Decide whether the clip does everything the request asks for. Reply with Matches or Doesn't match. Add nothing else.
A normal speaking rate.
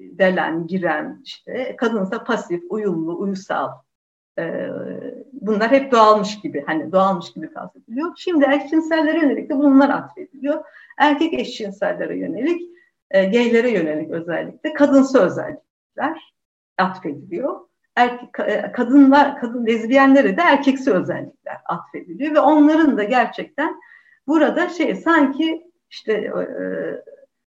Matches